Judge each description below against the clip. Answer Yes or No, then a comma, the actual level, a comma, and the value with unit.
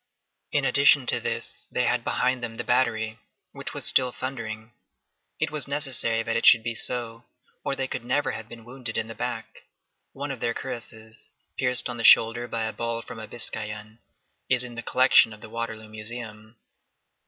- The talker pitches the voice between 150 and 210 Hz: No, low, 115 Hz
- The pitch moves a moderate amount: No, narrow, 2.2 semitones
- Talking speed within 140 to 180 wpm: No, average, 190 wpm